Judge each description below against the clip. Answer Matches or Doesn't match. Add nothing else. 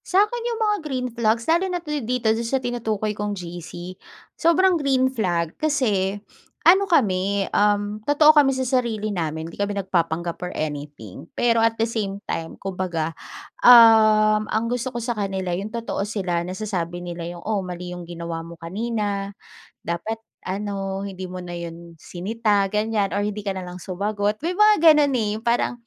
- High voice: Matches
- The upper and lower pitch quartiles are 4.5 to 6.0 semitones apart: Matches